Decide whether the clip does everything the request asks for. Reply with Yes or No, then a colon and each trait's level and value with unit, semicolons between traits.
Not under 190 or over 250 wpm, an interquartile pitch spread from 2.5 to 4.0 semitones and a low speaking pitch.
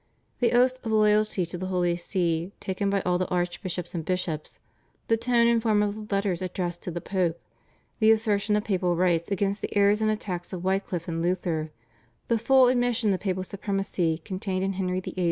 No: average, 195 wpm; average, 3.2 semitones; high, 190 Hz